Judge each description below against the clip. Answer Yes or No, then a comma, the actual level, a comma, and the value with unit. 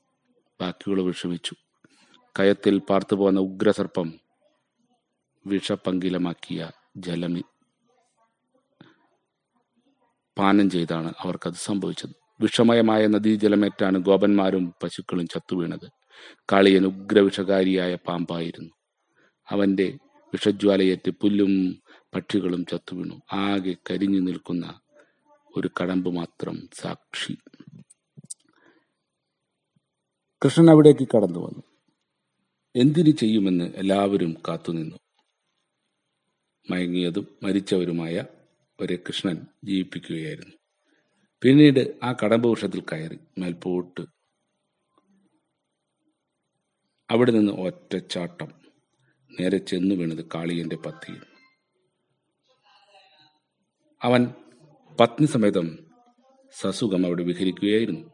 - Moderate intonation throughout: No, wide, 8.1 semitones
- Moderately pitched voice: No, low, 100 Hz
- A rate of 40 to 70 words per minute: Yes, average, 65 wpm